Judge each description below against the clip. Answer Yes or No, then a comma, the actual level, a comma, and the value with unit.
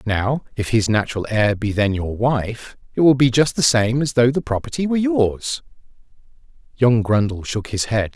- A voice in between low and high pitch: No, low, 120 Hz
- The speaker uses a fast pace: No, average, 190 wpm